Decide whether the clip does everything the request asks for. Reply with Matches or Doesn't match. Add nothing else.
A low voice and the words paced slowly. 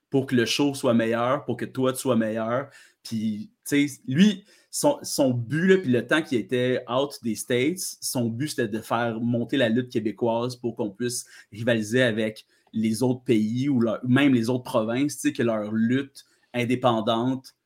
Doesn't match